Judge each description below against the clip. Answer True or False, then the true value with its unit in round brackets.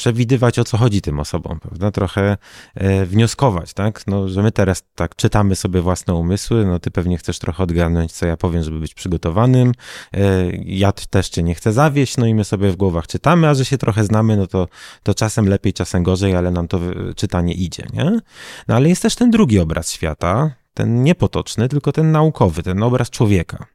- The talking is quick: True (200 wpm)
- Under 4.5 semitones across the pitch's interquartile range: False (4.8 semitones)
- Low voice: True (100 Hz)